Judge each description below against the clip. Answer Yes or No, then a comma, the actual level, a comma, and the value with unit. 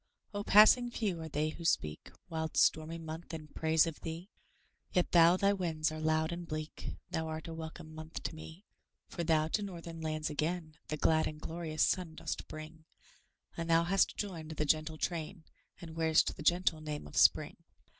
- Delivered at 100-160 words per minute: No, average, 185 wpm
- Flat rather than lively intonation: Yes, narrow, 1.6 semitones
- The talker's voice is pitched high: No, medium, 160 Hz